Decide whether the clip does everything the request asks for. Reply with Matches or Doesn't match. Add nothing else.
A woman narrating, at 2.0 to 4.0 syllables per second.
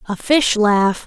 Matches